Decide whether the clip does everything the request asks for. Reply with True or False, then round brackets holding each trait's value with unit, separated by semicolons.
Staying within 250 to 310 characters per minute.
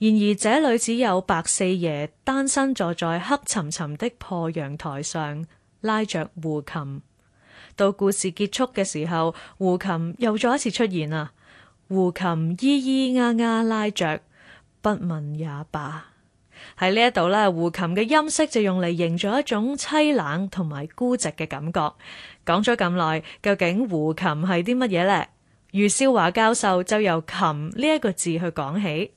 False (220 characters per minute)